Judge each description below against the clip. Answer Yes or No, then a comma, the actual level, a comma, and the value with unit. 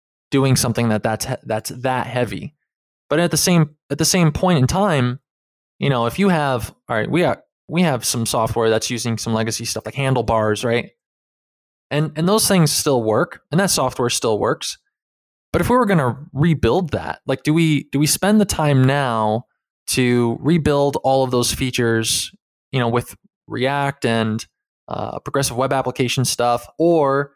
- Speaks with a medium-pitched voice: No, low, 130 Hz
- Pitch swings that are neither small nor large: Yes, average, 4.7 semitones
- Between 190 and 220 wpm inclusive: No, average, 180 wpm